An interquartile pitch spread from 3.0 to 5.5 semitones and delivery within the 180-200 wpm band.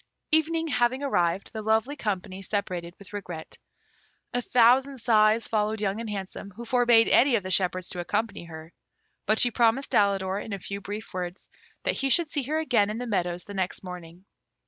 Yes: average, 4.4 semitones; average, 190 wpm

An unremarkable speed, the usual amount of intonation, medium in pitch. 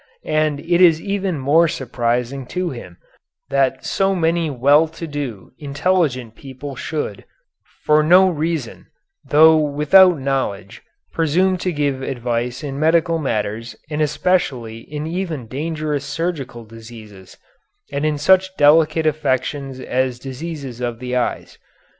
No: slow, 130 wpm; average, 4.5 semitones; medium, 145 Hz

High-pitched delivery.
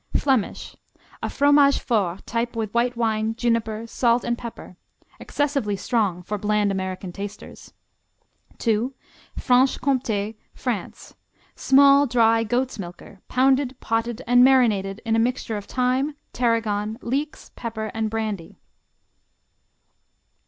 Yes: high, 230 Hz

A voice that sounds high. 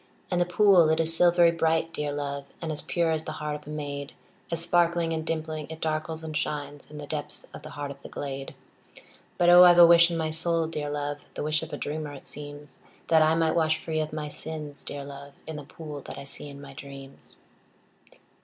No: medium, 155 Hz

